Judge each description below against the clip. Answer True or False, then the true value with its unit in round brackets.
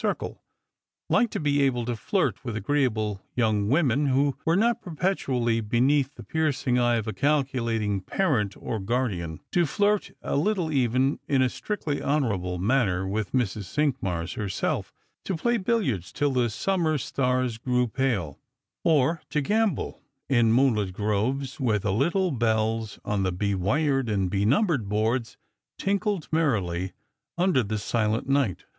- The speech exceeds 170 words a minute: False (150 wpm)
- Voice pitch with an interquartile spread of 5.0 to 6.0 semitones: True (5.6 semitones)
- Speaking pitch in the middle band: False (125 Hz)